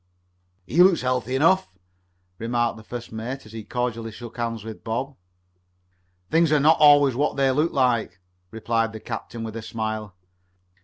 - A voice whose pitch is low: Yes, low, 120 Hz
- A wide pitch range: No, average, 3.4 semitones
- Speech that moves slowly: No, average, 160 wpm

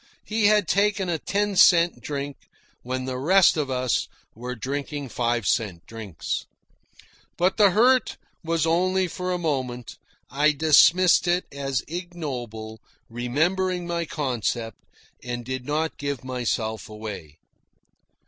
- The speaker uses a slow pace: Yes, slow, 130 wpm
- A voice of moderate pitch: Yes, medium, 145 Hz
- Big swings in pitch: Yes, wide, 6.4 semitones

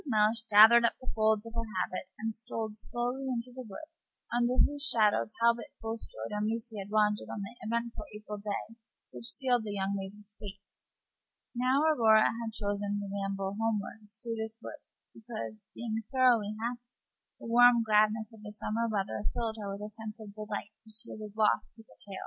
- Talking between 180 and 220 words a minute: Yes, average, 185 wpm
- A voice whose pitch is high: Yes, high, 220 Hz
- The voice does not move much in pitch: Yes, narrow, 2.0 semitones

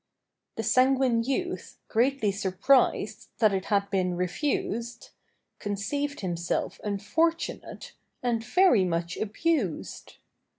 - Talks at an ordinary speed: No, slow, 95 wpm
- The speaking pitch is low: No, high, 225 Hz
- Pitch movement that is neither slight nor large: No, wide, 5.9 semitones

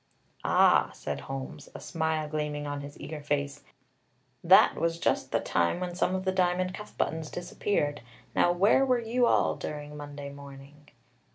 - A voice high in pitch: No, medium, 150 Hz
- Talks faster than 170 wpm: No, average, 165 wpm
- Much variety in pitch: No, average, 3.9 semitones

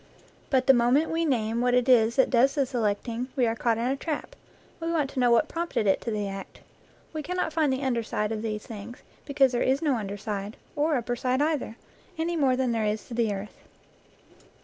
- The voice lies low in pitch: No, high, 245 Hz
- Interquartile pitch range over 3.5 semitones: Yes, average, 3.9 semitones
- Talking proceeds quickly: Yes, fast, 225 wpm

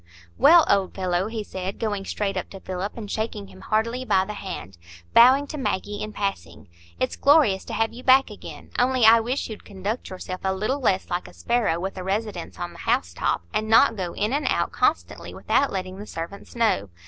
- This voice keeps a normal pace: No, fast, 210 wpm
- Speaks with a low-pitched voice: No, high, 205 Hz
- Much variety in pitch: No, average, 3.6 semitones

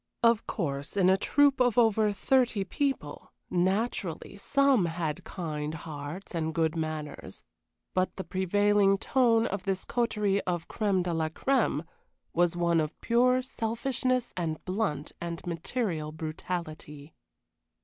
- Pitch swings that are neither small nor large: No, wide, 5.8 semitones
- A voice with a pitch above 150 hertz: Yes, medium, 185 Hz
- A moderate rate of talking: No, slow, 130 wpm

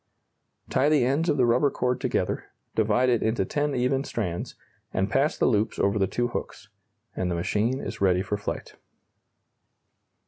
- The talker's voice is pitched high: No, low, 120 Hz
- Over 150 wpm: Yes, average, 170 wpm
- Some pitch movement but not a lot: Yes, average, 4.6 semitones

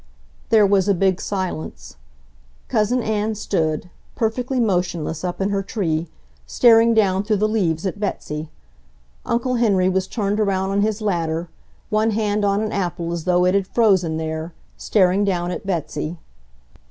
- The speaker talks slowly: No, average, 155 wpm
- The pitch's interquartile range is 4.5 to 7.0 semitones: No, average, 3.5 semitones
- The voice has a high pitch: Yes, high, 195 Hz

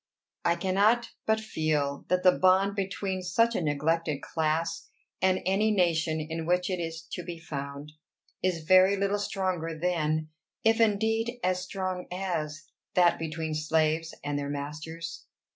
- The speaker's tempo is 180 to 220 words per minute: No, average, 145 wpm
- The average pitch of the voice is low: No, medium, 175 Hz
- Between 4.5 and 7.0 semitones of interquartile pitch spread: No, average, 3.2 semitones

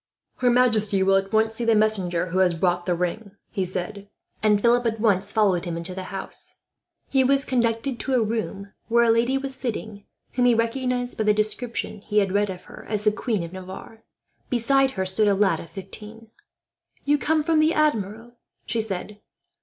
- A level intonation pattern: No, average, 3.6 semitones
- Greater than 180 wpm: Yes, average, 200 wpm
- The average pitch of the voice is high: Yes, high, 215 Hz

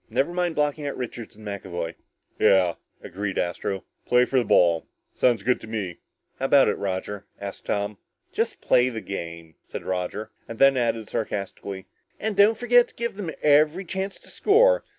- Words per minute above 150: Yes, average, 175 wpm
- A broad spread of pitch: Yes, wide, 7.6 semitones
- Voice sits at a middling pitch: No, low, 115 Hz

